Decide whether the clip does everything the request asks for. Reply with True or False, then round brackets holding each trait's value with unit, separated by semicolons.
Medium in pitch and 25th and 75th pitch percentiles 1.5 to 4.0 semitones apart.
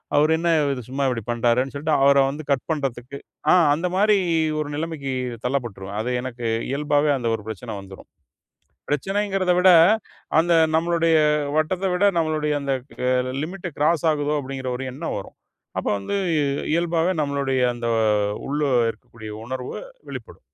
False (145 Hz; 4.5 semitones)